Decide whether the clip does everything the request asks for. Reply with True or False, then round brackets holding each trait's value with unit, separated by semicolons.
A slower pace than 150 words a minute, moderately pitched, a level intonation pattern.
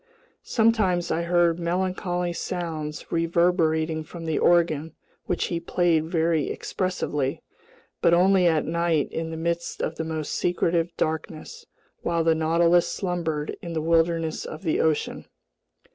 True (135 wpm; 170 Hz; 1.6 semitones)